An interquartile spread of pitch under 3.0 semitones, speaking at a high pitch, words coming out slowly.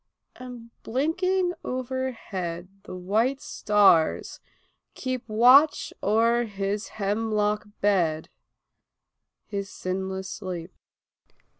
No: average, 4.7 semitones; high, 215 Hz; slow, 80 wpm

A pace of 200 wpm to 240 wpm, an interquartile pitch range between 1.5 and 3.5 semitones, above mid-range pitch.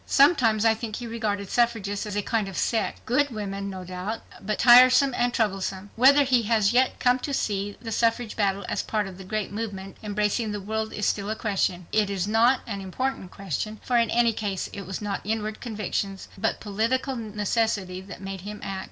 Yes: fast, 205 wpm; average, 2.8 semitones; high, 215 Hz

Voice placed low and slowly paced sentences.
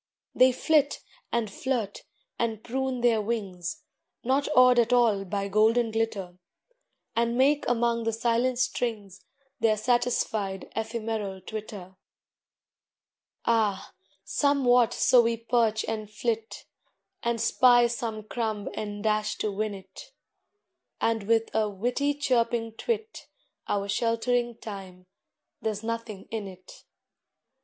No: high, 225 Hz; slow, 115 wpm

